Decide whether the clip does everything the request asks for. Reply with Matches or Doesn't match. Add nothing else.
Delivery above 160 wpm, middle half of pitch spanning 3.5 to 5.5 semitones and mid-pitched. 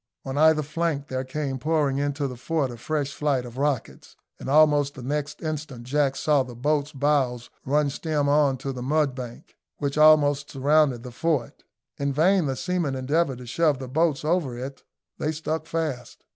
Doesn't match